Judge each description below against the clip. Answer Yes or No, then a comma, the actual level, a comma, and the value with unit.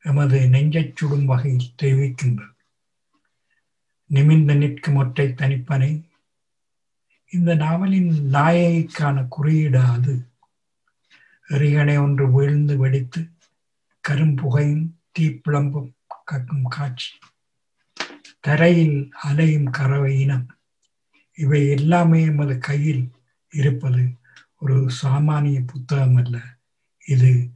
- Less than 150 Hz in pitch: Yes, medium, 140 Hz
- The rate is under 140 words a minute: Yes, average, 80 wpm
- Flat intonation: Yes, narrow, 2.3 semitones